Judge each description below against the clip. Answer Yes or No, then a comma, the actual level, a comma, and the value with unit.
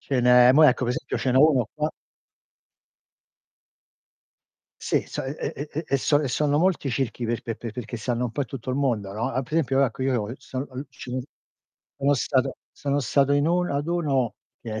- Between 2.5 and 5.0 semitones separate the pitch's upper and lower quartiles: Yes, average, 2.8 semitones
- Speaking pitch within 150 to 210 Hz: No, low, 135 Hz